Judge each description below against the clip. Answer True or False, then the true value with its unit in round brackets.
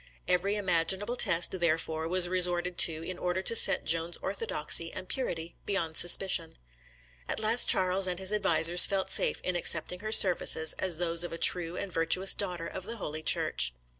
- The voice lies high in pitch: False (180 Hz)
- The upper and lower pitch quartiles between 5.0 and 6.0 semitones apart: False (2.4 semitones)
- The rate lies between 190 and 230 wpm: False (175 wpm)